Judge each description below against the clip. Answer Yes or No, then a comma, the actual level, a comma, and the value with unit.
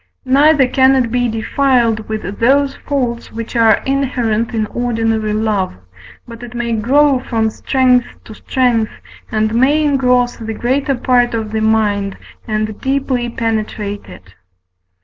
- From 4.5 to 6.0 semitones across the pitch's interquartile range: No, average, 3.0 semitones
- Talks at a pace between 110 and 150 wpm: Yes, average, 140 wpm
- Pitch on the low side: No, high, 235 Hz